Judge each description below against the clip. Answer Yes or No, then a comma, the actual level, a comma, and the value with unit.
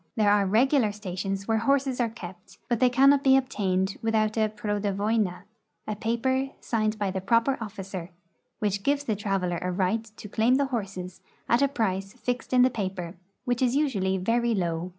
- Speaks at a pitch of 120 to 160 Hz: No, high, 215 Hz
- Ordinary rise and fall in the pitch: Yes, average, 4.1 semitones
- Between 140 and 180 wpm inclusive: No, average, 190 wpm